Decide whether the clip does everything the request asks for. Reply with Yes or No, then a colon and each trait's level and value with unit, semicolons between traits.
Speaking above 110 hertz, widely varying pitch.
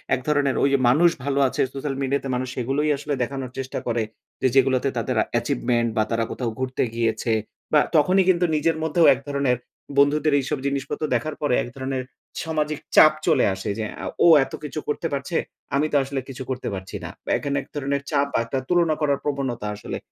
No: medium, 140 Hz; average, 2.7 semitones